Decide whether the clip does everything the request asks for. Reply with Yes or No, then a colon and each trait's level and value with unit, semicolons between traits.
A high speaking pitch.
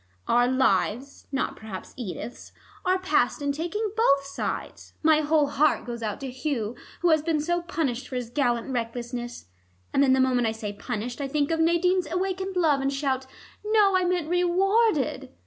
Yes: very high, 280 Hz